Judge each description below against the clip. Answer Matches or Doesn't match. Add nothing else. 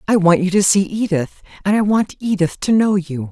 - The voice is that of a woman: Matches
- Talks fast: Matches